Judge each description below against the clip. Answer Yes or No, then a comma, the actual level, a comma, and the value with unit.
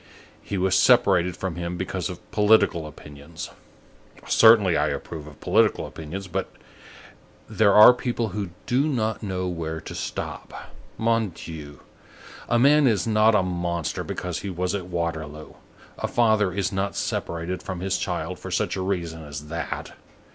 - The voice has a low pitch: Yes, very low, 95 Hz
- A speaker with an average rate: Yes, average, 155 wpm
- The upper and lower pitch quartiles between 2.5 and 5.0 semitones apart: Yes, average, 4.1 semitones